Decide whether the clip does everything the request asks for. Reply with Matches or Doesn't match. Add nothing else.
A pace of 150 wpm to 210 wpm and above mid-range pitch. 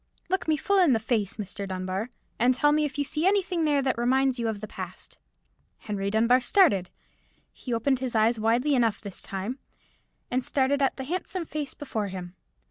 Matches